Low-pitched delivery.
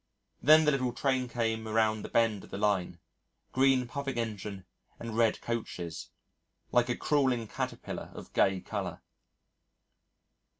Yes: low, 115 Hz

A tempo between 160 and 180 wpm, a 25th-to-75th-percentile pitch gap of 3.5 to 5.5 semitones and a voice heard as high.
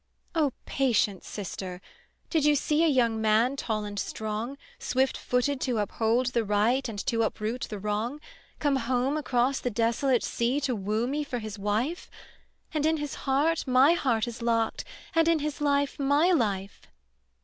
Yes: average, 170 wpm; average, 4.5 semitones; very high, 250 Hz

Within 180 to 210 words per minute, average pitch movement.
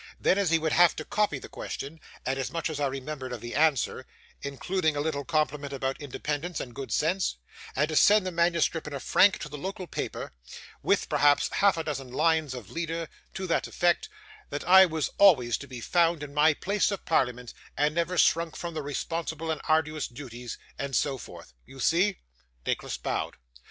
Yes: average, 195 wpm; average, 3.5 semitones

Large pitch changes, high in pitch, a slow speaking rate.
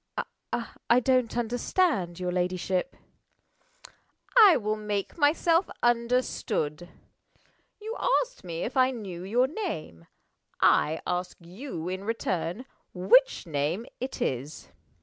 Yes: wide, 6.5 semitones; high, 215 Hz; slow, 110 wpm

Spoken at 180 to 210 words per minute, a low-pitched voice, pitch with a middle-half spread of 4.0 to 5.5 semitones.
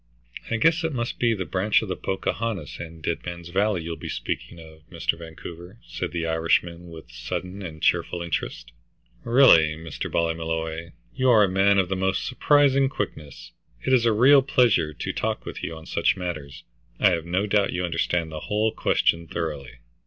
Yes: average, 185 wpm; very low, 90 Hz; average, 4.6 semitones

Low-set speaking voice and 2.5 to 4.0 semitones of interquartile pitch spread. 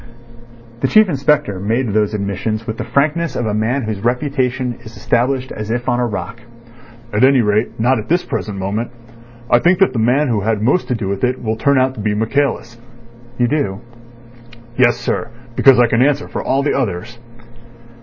Yes: low, 120 Hz; average, 3.6 semitones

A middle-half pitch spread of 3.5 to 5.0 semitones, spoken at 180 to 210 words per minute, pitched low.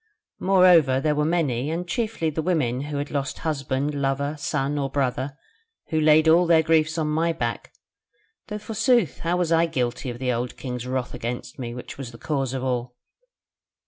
No: average, 4.1 semitones; average, 185 wpm; medium, 145 Hz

